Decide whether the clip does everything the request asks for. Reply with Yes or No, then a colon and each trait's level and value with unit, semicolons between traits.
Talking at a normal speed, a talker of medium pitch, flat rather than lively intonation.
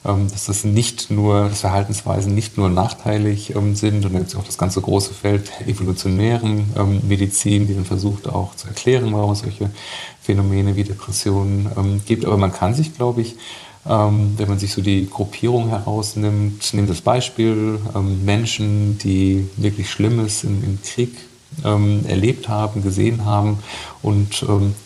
No: average, 140 wpm; low, 105 Hz; narrow, 1.4 semitones